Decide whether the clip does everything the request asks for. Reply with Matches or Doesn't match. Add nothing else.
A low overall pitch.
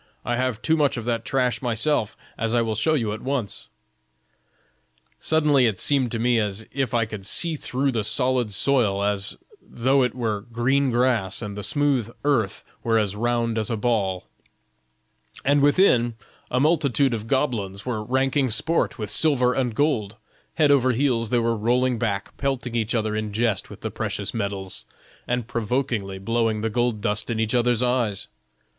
Matches